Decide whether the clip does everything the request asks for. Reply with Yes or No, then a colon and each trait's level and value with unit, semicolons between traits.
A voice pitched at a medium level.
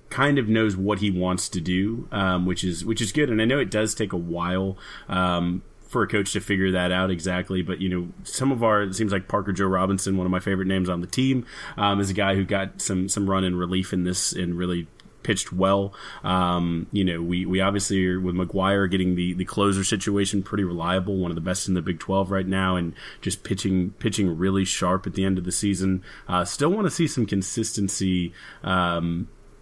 No: very low, 95 Hz